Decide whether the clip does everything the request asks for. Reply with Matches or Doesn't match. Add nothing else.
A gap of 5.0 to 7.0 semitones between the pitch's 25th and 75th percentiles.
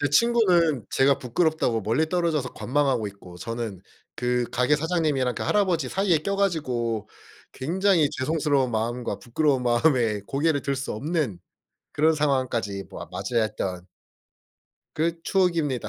Matches